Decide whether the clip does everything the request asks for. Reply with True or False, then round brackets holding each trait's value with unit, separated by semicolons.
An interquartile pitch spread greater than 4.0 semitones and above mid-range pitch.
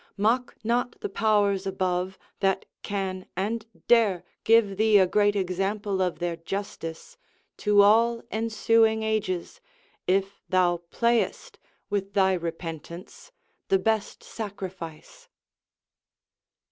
False (2.9 semitones; 200 Hz)